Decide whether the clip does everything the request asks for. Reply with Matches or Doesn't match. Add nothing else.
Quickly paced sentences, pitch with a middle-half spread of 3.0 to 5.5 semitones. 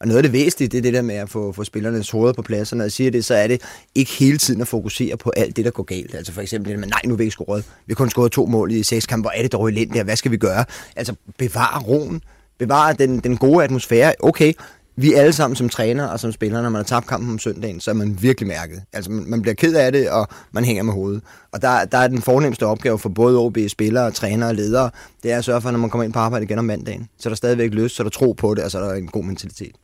Doesn't match